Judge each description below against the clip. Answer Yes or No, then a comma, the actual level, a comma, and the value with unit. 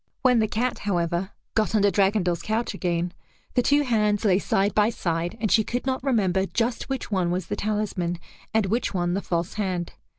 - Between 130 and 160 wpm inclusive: No, average, 195 wpm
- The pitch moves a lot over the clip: No, average, 3.8 semitones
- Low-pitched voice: No, high, 205 Hz